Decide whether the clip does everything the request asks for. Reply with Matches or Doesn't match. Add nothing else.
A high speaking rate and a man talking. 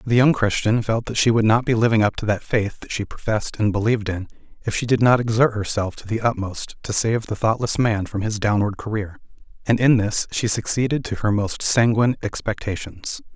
Matches